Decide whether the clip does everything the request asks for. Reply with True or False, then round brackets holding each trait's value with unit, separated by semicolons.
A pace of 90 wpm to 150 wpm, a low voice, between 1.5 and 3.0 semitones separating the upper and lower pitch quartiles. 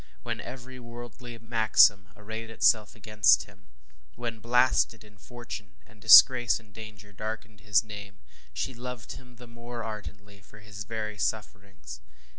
True (145 wpm; 110 Hz; 2.5 semitones)